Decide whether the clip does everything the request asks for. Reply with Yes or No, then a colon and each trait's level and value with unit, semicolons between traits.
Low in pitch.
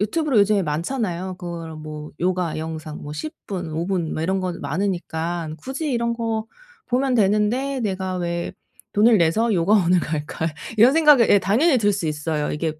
No: medium, 185 Hz